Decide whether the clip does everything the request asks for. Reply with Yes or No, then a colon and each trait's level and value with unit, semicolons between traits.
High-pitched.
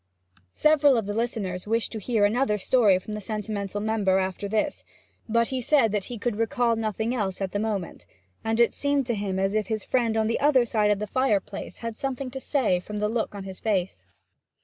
Yes: high, 220 Hz